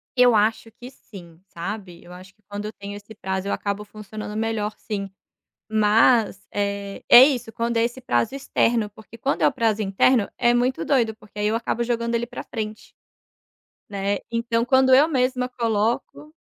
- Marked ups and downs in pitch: No, average, 2.8 semitones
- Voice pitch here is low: No, high, 220 Hz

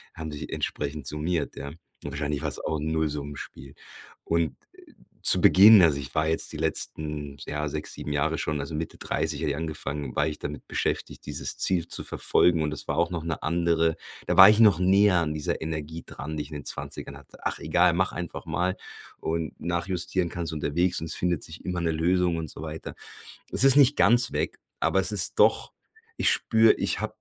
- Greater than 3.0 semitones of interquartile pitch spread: No, average, 2.7 semitones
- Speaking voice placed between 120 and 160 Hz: No, very low, 80 Hz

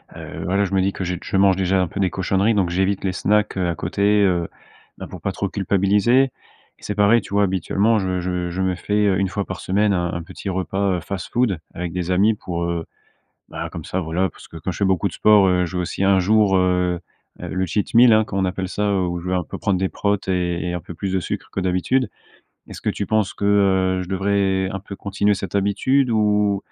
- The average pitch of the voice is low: Yes, very low, 95 Hz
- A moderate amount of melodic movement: No, narrow, 1.9 semitones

